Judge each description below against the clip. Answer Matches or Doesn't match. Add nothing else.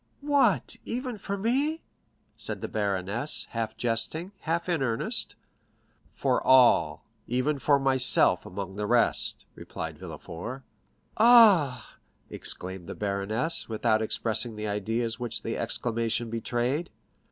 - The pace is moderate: Doesn't match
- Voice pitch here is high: Doesn't match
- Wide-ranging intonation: Matches